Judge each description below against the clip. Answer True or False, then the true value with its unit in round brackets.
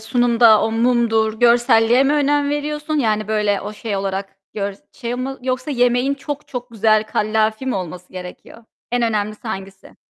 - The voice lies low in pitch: False (225 Hz)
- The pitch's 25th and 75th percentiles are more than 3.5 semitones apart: False (3.0 semitones)